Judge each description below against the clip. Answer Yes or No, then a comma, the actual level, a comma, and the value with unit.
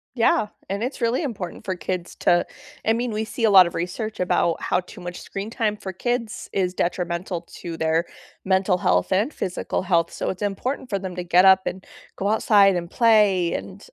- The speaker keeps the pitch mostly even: No, average, 3.5 semitones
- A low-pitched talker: No, high, 190 Hz